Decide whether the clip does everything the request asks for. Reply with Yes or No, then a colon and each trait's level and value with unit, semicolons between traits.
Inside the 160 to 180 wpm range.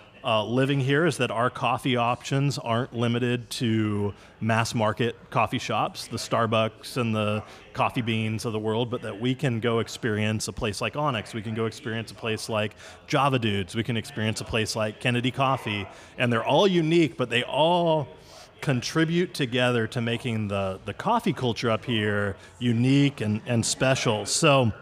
Yes: average, 175 wpm